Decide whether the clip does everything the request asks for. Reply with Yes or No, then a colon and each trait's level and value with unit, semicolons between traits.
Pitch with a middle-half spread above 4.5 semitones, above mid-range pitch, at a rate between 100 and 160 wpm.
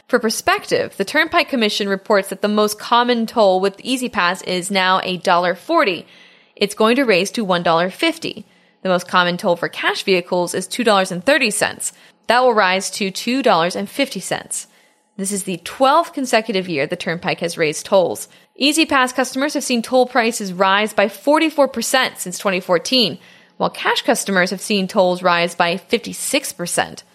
Yes: wide, 5.4 semitones; high, 205 Hz; average, 150 wpm